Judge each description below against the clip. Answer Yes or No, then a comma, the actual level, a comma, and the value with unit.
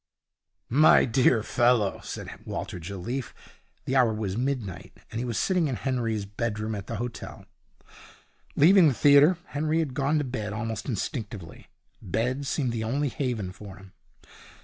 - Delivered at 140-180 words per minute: Yes, average, 150 wpm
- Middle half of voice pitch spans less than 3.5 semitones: No, average, 4.5 semitones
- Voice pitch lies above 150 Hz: No, low, 120 Hz